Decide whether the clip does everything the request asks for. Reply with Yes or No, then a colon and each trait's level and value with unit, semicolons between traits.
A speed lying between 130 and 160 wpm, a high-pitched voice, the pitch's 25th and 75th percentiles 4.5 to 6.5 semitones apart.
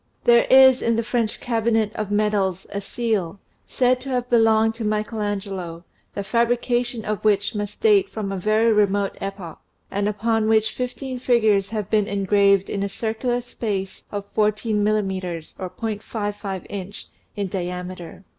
No: average, 155 wpm; high, 210 Hz; narrow, 2.6 semitones